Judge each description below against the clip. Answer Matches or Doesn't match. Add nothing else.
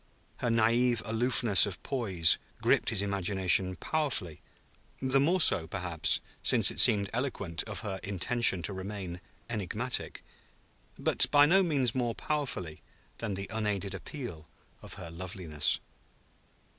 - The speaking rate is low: Matches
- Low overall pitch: Matches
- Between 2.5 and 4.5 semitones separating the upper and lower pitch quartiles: Doesn't match